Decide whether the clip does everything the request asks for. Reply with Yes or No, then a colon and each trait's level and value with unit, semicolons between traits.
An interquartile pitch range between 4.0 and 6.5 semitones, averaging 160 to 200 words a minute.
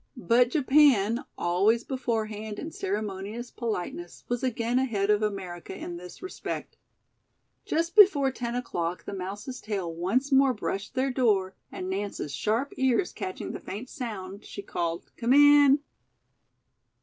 No: average, 5.1 semitones; slow, 135 wpm